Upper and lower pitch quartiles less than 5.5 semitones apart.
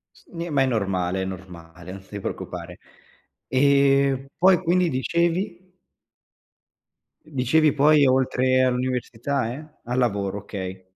No: wide, 6.8 semitones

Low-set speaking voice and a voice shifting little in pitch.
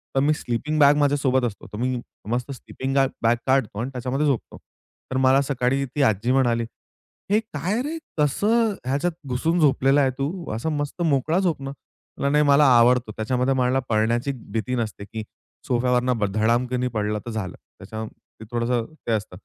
No: low, 130 Hz; average, 3.4 semitones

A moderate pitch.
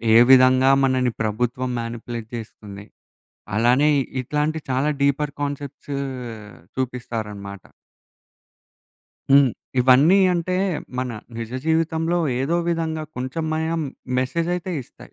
No: low, 130 Hz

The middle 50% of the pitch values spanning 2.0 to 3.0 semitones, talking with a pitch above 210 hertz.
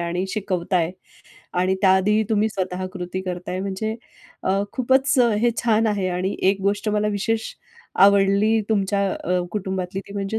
No: narrow, 2.4 semitones; high, 200 Hz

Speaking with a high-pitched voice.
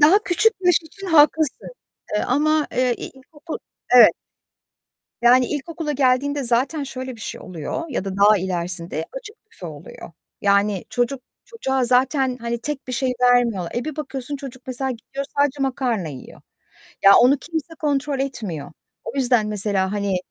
Yes: very high, 260 Hz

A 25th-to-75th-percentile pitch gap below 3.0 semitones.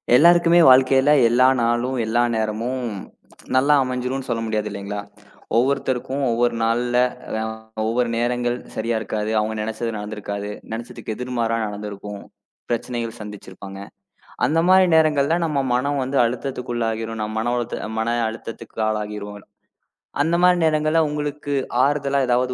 No: average, 3.6 semitones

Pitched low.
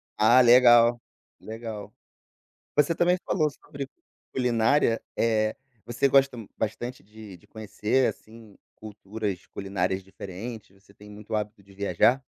Yes: low, 110 Hz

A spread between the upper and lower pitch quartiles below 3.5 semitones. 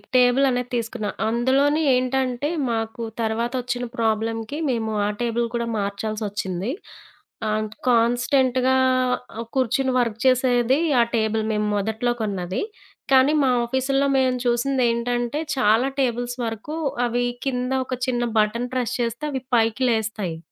Yes: narrow, 2.5 semitones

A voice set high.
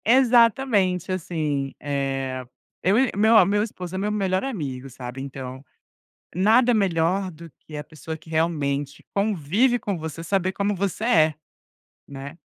No: medium, 175 Hz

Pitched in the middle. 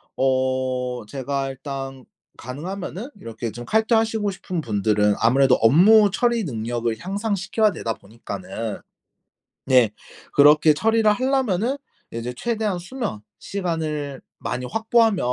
Yes: medium, 150 Hz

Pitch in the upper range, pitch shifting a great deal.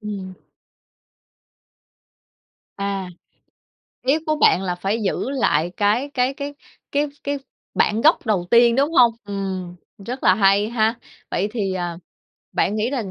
No: high, 215 Hz; average, 4.6 semitones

